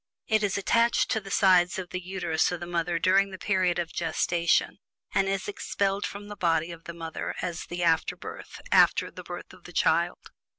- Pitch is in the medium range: Yes, medium, 180 Hz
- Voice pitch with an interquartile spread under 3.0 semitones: Yes, narrow, 2.5 semitones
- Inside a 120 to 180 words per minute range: No, average, 200 wpm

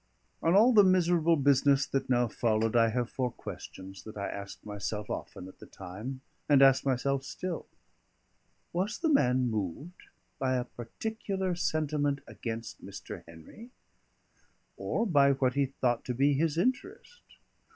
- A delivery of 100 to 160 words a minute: Yes, average, 150 wpm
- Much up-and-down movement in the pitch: Yes, wide, 6.5 semitones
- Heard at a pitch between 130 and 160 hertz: Yes, low, 135 Hz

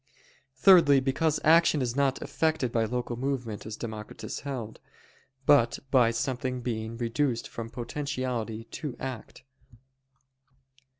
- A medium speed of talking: No, slow, 115 wpm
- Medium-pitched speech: No, low, 125 Hz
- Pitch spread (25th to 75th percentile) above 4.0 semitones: No, average, 3.5 semitones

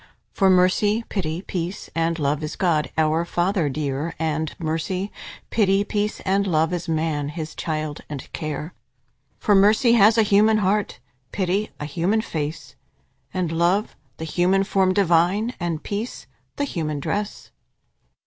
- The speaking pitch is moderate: Yes, medium, 175 Hz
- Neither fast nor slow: Yes, average, 145 wpm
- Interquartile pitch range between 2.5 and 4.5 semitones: Yes, average, 4.2 semitones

